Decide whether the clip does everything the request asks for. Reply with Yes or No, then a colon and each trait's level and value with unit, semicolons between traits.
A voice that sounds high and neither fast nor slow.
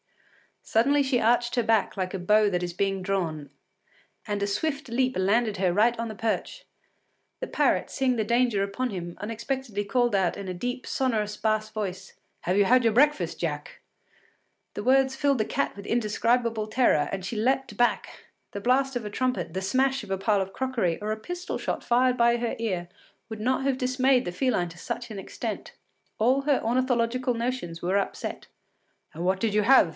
Yes: high, 225 Hz; average, 195 wpm